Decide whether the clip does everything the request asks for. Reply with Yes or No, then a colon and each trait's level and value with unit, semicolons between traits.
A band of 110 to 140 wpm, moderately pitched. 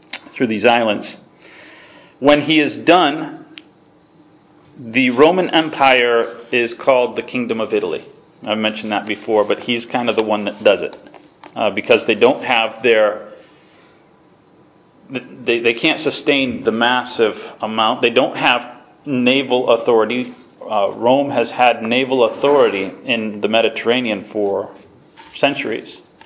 No: slow, 135 wpm; low, 125 Hz